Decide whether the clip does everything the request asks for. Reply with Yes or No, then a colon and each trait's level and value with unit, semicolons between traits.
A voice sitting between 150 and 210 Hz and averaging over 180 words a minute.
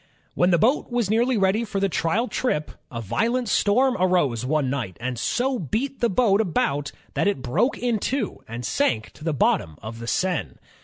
Yes: medium, 185 Hz; average, 195 wpm